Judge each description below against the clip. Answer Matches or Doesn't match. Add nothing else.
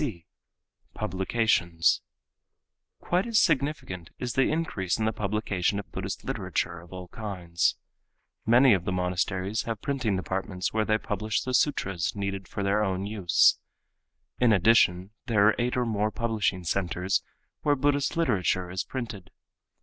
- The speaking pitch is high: Doesn't match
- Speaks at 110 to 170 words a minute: Matches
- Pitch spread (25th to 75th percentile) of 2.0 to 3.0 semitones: Doesn't match